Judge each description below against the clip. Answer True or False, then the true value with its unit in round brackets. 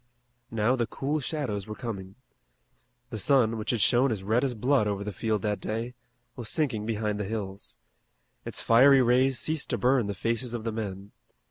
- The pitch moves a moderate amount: True (3.4 semitones)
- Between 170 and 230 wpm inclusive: True (190 wpm)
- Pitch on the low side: True (115 Hz)